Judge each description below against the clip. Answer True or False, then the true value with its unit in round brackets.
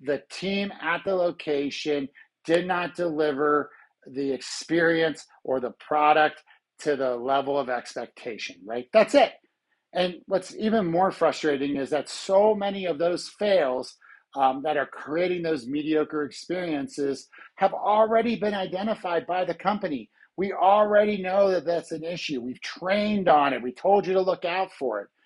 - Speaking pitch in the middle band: True (165 Hz)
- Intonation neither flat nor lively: True (5.0 semitones)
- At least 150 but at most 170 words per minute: True (155 wpm)